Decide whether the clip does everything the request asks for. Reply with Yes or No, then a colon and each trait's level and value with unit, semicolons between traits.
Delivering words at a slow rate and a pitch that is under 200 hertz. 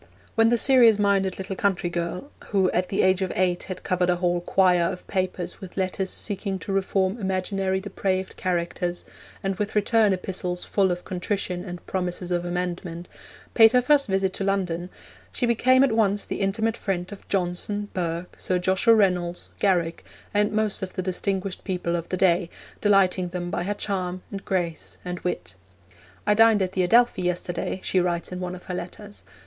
No: average, 185 wpm; medium, 185 Hz